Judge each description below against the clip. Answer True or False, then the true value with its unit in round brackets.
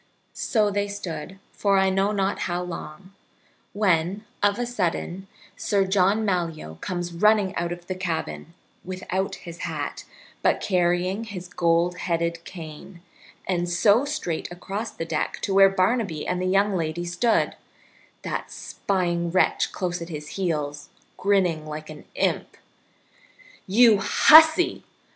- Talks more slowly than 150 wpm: True (140 wpm)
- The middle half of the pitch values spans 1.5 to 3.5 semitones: True (2.9 semitones)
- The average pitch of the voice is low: False (185 Hz)